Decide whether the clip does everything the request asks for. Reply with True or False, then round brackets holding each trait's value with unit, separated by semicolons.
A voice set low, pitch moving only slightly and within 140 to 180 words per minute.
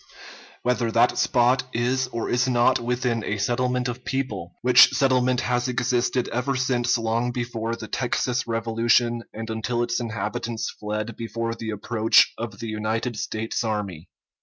True (120 Hz; 1.8 semitones; 155 wpm)